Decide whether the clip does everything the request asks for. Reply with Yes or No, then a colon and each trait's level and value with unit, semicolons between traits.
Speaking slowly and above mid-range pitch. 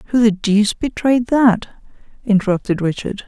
Yes: slow, 130 wpm; high, 220 Hz